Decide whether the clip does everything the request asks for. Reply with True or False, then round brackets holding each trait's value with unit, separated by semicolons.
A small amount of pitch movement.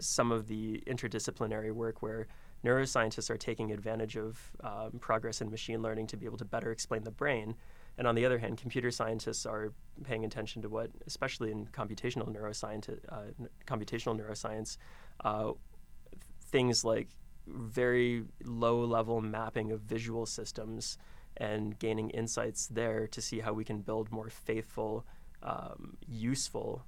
True (1.2 semitones)